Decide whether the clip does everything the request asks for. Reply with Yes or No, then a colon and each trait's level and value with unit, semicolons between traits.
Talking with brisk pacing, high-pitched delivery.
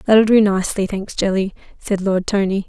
No: average, 180 wpm; high, 200 Hz